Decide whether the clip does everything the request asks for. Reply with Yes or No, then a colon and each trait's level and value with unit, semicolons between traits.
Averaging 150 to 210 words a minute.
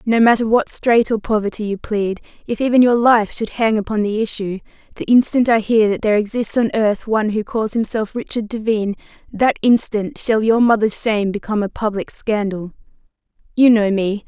Yes: average, 180 wpm